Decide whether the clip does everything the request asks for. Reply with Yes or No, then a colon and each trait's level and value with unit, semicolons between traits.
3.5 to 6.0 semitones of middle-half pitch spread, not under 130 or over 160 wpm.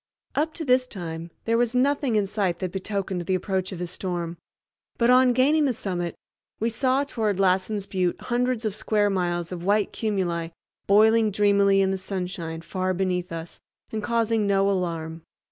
No: average, 4.0 semitones; average, 175 wpm